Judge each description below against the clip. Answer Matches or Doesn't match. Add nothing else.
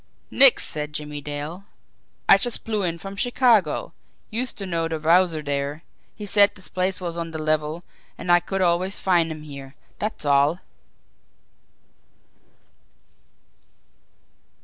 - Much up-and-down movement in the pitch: Doesn't match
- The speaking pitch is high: Doesn't match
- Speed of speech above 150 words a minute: Doesn't match